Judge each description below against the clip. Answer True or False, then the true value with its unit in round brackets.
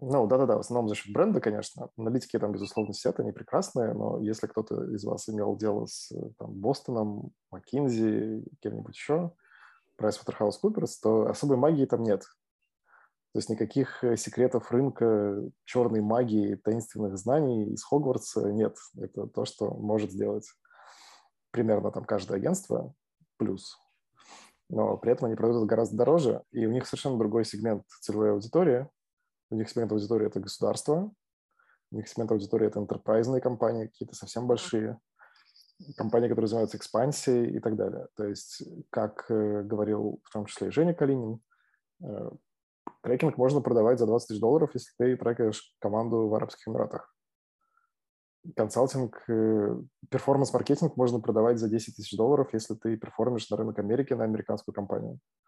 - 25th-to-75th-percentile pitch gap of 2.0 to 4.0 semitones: True (2.9 semitones)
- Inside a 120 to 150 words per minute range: True (145 wpm)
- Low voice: True (115 Hz)